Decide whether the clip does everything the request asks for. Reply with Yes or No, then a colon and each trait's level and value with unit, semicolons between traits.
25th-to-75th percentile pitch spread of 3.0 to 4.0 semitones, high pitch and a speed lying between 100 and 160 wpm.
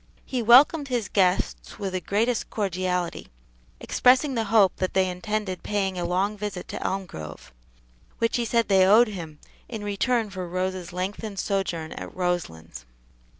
Yes: average, 3.4 semitones; high, 195 Hz; average, 150 wpm